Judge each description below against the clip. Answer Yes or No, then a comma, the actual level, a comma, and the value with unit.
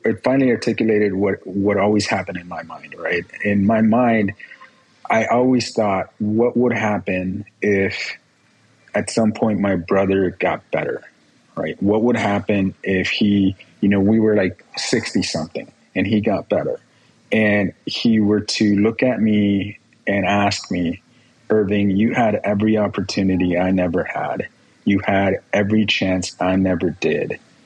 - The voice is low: Yes, low, 105 Hz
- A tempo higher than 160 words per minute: No, average, 150 wpm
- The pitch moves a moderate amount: No, narrow, 2.1 semitones